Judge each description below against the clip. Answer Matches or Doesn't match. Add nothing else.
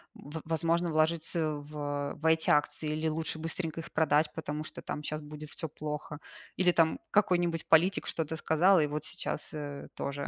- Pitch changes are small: Matches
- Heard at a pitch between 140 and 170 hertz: Matches